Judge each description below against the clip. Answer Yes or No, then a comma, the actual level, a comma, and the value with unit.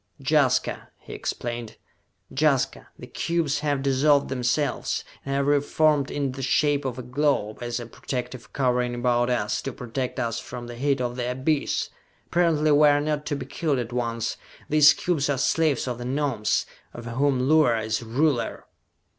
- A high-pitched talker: No, low, 135 Hz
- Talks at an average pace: Yes, average, 170 wpm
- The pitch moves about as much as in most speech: Yes, average, 3.2 semitones